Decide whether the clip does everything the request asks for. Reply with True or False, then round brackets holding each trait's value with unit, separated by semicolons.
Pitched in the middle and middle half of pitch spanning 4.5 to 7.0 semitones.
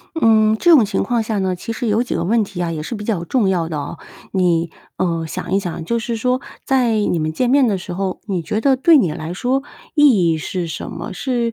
False (205 Hz; 5.6 semitones)